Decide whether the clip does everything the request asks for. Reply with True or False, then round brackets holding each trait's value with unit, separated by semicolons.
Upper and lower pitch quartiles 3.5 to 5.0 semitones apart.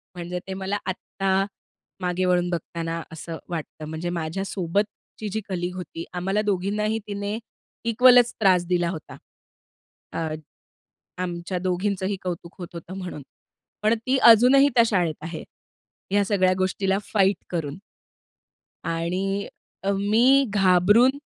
False (2.8 semitones)